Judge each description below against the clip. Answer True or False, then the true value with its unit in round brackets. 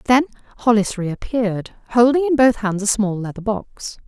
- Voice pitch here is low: False (225 Hz)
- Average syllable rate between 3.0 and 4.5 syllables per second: False (4.9 syllables/s)